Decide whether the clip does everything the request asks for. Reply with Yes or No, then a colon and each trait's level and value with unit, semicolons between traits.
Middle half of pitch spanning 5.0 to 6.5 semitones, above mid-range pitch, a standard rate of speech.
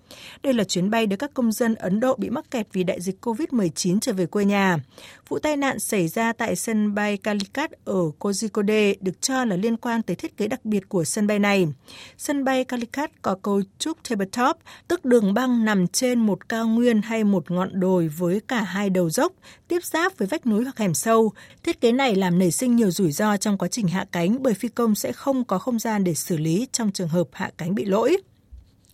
No: average, 4.5 semitones; high, 215 Hz; average, 230 wpm